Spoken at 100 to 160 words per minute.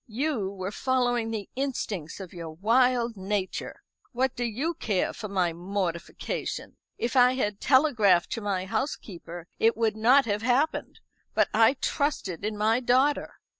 Yes: average, 150 wpm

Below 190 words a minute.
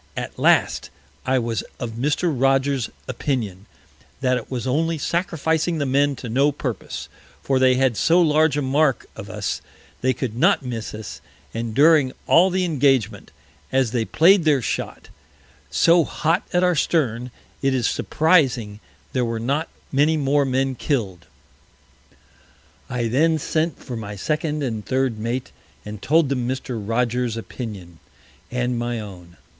Yes: average, 150 wpm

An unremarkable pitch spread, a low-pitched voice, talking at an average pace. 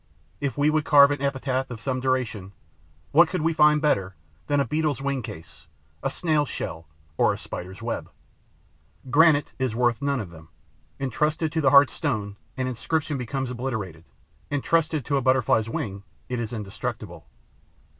Yes: average, 4.5 semitones; low, 130 Hz; average, 165 wpm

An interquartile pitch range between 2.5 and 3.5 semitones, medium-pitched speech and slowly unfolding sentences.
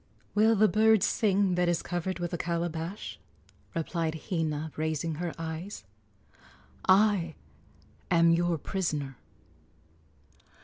Yes: average, 2.9 semitones; medium, 170 Hz; slow, 105 wpm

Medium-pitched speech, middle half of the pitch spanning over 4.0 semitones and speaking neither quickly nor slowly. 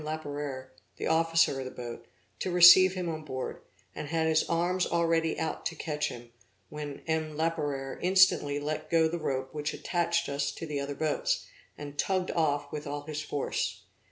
No: medium, 155 Hz; narrow, 2.5 semitones; average, 180 wpm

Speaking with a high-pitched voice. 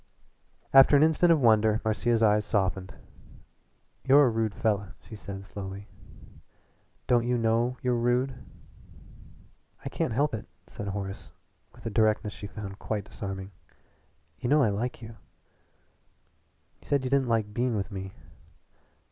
No: low, 110 Hz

